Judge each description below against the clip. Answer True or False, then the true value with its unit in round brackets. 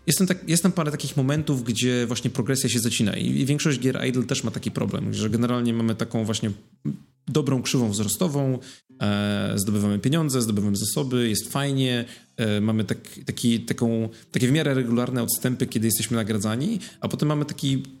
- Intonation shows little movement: False (3.7 semitones)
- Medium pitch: False (125 Hz)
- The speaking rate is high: True (175 wpm)